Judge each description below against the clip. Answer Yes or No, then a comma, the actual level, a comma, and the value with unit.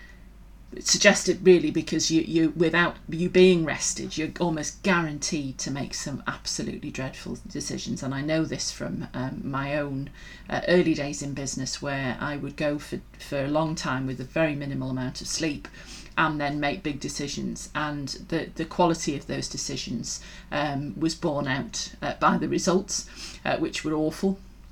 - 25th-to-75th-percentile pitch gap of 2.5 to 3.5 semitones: Yes, average, 2.9 semitones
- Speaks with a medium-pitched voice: Yes, medium, 155 Hz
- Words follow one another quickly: No, average, 170 wpm